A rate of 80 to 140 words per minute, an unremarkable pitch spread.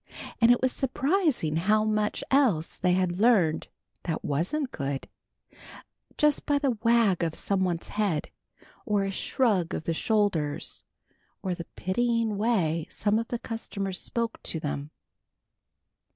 No: slow, 135 wpm; wide, 5.7 semitones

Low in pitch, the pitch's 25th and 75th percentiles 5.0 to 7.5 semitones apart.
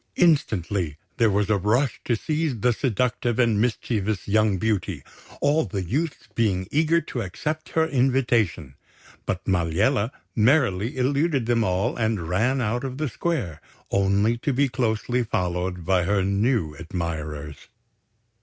Yes: low, 110 Hz; wide, 5.5 semitones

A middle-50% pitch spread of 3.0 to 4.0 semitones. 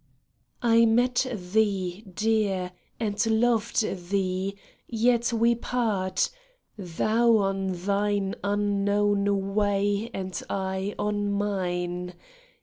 No: narrow, 2.5 semitones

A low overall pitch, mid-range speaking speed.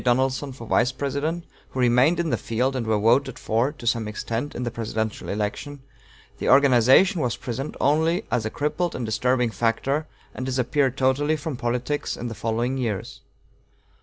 Yes: low, 130 Hz; average, 170 wpm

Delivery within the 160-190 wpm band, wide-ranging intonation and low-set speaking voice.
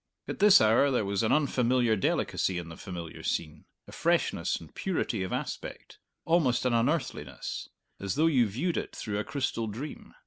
Yes: average, 175 wpm; wide, 6.3 semitones; low, 115 Hz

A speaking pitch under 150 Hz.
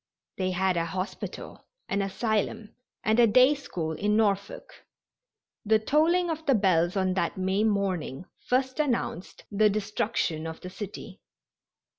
No: high, 200 Hz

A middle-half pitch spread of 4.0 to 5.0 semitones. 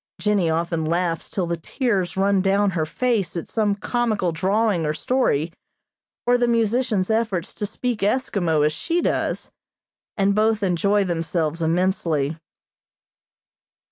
Yes: average, 4.7 semitones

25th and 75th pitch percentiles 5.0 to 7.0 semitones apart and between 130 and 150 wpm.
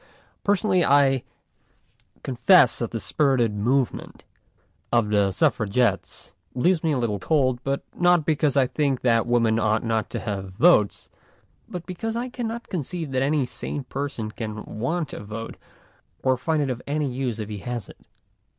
No: average, 5.3 semitones; average, 160 wpm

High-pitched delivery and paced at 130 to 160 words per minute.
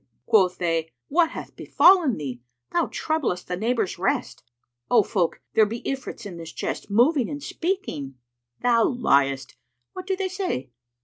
Yes: high, 230 Hz; average, 150 wpm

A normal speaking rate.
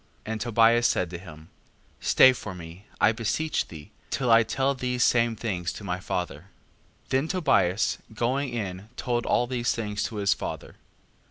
Yes: average, 175 wpm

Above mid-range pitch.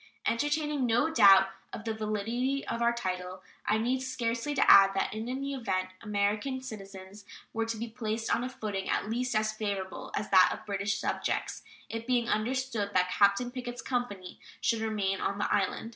Yes: high, 220 Hz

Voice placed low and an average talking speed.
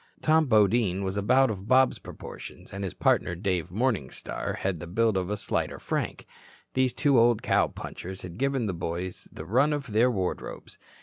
Yes: low, 105 Hz; average, 180 wpm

